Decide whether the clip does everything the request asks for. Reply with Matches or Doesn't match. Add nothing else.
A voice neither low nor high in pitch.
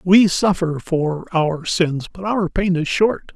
Matches